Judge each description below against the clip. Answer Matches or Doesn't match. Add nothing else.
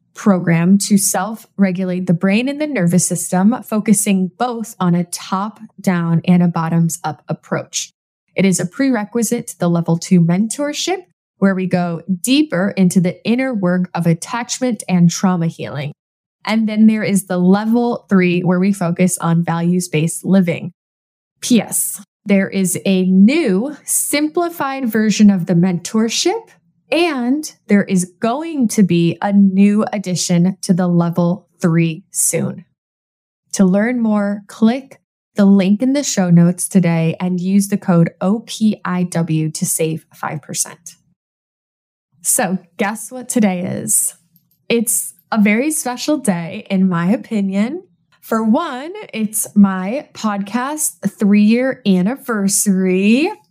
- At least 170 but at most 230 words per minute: Doesn't match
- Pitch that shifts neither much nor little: Matches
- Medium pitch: Doesn't match